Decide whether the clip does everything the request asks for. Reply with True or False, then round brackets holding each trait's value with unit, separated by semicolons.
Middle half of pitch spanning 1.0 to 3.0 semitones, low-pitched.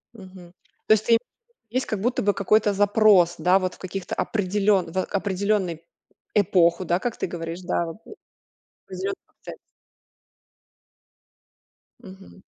False (2.7 semitones; 190 Hz)